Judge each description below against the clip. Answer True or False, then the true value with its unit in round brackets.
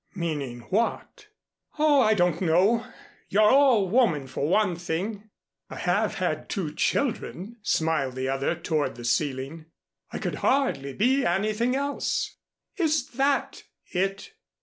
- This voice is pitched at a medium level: False (195 Hz)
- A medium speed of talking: False (130 wpm)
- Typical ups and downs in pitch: False (7.4 semitones)